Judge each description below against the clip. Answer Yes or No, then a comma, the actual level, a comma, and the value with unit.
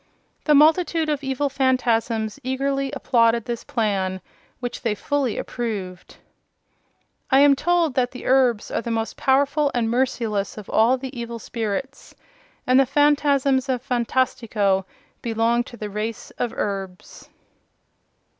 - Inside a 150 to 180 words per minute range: No, slow, 135 wpm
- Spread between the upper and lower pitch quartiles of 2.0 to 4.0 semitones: Yes, average, 3.4 semitones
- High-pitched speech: Yes, high, 245 Hz